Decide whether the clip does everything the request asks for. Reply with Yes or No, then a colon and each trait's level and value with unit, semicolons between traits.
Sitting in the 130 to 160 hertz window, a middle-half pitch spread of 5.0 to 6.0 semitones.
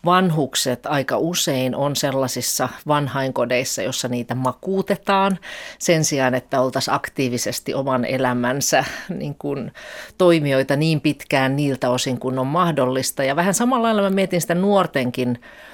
Yes: medium, 140 Hz; wide, 5.5 semitones